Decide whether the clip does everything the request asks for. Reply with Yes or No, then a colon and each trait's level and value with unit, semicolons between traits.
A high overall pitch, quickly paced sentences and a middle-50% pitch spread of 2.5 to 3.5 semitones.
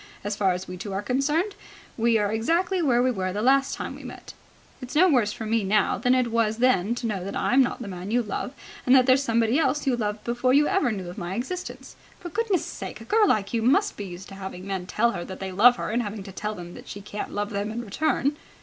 No: high, 230 Hz; fast, 265 wpm; average, 4.5 semitones